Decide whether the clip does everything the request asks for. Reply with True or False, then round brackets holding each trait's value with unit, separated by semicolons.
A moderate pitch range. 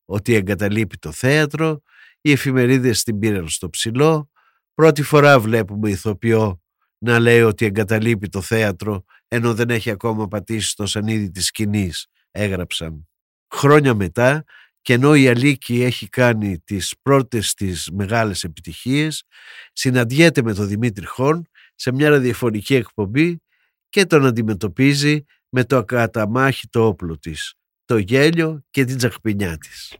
True (4.6 semitones)